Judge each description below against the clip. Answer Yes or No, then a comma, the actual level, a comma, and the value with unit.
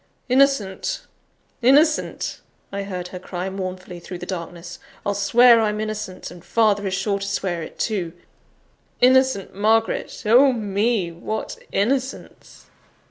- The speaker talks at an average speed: No, slow, 130 wpm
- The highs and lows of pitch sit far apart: No, average, 3.9 semitones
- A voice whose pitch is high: Yes, high, 200 Hz